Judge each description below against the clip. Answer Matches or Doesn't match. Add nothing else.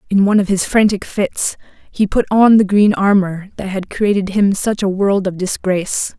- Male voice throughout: Doesn't match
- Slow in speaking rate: Doesn't match